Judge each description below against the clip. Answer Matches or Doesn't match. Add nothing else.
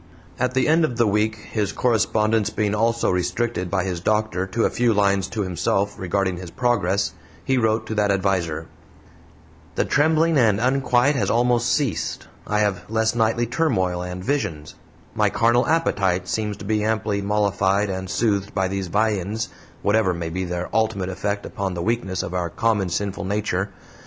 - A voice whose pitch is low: Matches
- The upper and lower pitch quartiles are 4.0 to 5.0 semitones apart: Doesn't match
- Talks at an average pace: Matches